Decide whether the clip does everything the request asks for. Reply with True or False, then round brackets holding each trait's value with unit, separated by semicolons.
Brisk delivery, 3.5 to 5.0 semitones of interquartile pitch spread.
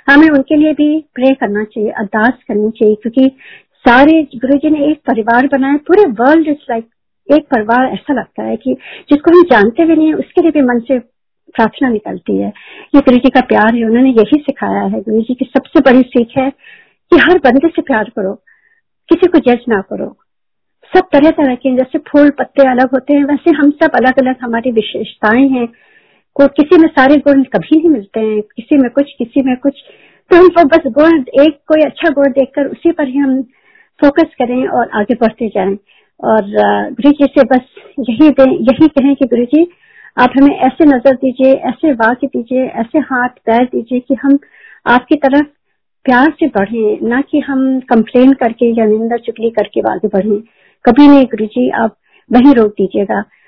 True (195 wpm; 4.1 semitones)